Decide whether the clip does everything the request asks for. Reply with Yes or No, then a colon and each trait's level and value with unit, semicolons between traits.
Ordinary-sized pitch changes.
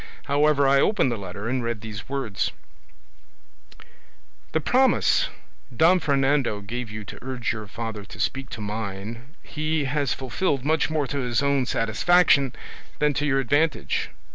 Yes: average, 4.6 semitones